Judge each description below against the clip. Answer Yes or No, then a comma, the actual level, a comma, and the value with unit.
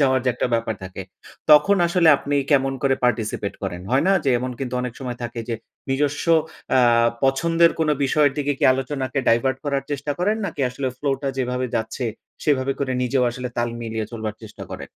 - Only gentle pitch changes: No, average, 3.0 semitones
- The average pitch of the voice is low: Yes, low, 130 Hz